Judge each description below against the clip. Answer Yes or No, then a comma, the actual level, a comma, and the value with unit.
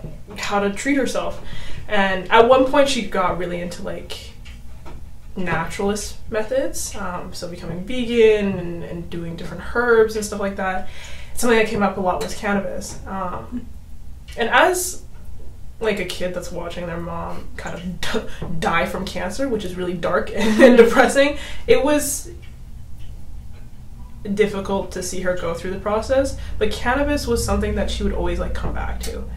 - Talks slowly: No, average, 165 wpm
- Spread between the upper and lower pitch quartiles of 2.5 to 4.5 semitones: No, average, 4.9 semitones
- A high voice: Yes, high, 200 Hz